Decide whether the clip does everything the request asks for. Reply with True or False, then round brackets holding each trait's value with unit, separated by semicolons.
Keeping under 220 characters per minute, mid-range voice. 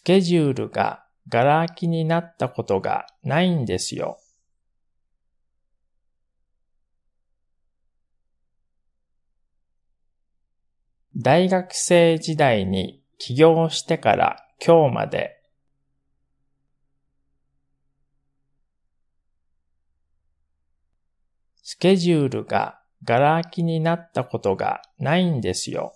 False (150 characters per minute; 105 Hz)